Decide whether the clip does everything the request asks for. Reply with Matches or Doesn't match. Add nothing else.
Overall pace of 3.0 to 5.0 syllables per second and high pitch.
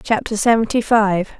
Matches